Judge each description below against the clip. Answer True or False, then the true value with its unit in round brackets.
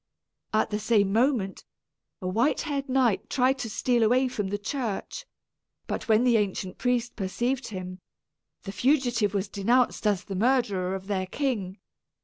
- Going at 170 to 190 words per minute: False (155 wpm)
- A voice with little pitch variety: False (4.4 semitones)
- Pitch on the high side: True (220 Hz)